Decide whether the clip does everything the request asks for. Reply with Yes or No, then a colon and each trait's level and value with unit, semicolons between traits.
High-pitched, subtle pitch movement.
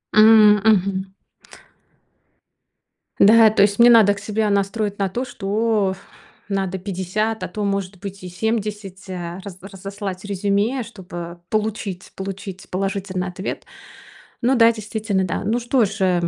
Yes: high, 200 Hz; narrow, 2.3 semitones